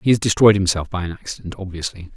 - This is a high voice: No, very low, 95 Hz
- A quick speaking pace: Yes, fast, 220 wpm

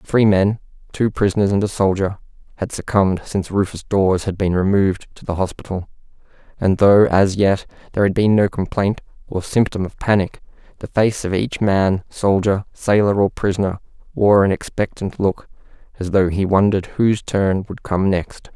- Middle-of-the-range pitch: No, low, 100 Hz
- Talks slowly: No, average, 165 wpm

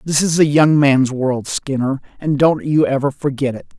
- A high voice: No, medium, 140 Hz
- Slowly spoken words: No, fast, 205 wpm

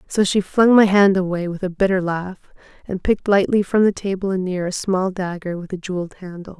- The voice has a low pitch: No, high, 190 Hz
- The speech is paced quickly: Yes, fast, 220 wpm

